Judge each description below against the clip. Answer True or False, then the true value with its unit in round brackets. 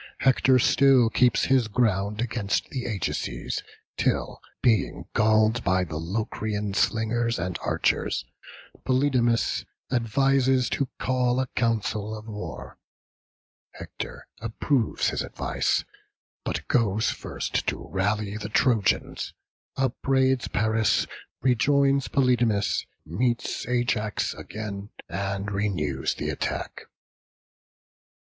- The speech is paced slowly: True (100 wpm)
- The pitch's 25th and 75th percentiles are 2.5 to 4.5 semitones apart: True (3.5 semitones)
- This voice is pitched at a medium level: False (110 Hz)